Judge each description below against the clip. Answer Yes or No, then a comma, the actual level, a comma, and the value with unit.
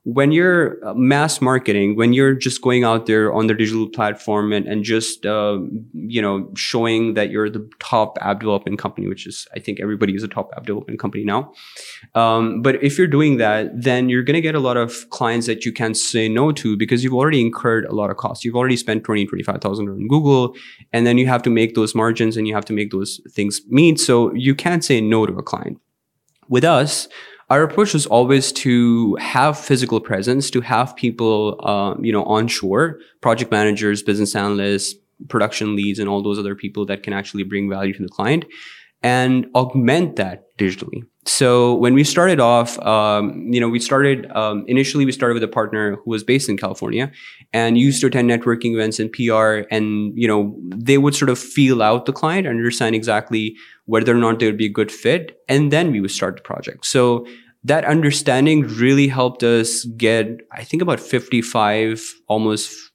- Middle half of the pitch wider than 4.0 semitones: No, average, 3.2 semitones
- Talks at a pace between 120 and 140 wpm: No, average, 200 wpm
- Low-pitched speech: Yes, low, 115 Hz